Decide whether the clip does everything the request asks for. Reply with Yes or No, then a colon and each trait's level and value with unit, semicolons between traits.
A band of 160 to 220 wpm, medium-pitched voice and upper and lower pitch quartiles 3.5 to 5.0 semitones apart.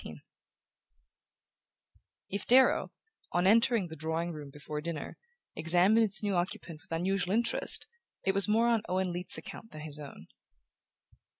No: average, 140 wpm; medium, 180 Hz; average, 4.7 semitones